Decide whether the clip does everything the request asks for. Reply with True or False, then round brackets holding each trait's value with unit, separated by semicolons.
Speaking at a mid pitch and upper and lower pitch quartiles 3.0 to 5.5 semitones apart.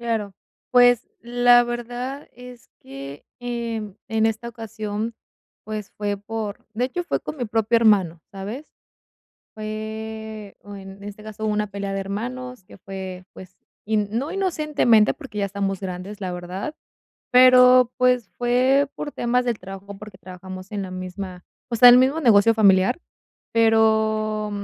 False (220 Hz; 3.5 semitones)